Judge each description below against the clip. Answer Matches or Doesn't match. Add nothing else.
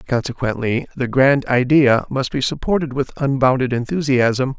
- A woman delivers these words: Doesn't match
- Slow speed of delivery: Matches